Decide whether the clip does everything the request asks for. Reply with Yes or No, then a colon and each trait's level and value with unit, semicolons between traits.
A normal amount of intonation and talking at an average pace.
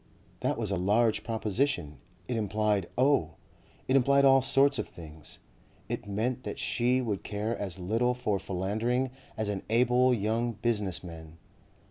Yes: average, 4.2 semitones; average, 150 wpm